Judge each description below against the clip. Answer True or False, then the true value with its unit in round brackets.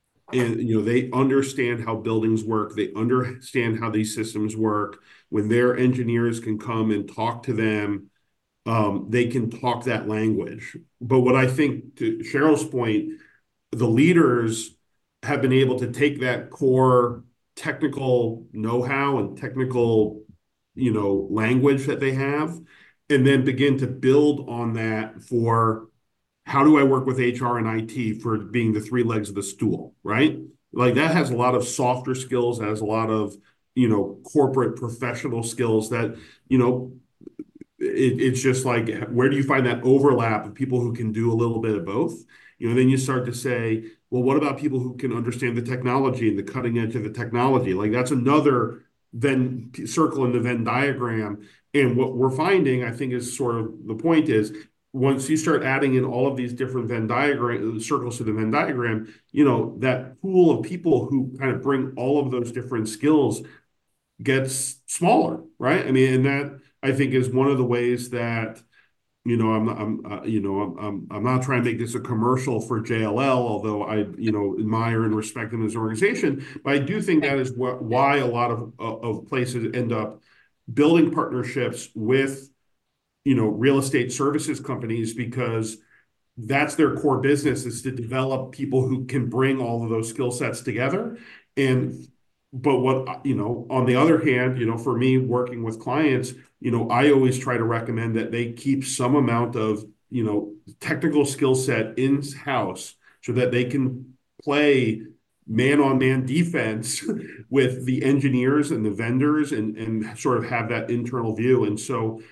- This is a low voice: True (125 Hz)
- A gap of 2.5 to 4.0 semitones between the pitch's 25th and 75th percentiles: True (3.1 semitones)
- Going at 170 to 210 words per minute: True (185 wpm)